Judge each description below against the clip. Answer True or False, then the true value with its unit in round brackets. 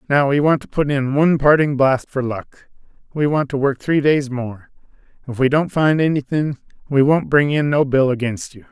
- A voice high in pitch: False (140 Hz)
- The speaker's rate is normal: False (215 wpm)